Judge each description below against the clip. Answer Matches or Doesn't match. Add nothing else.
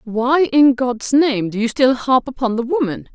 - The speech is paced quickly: Matches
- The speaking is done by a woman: Matches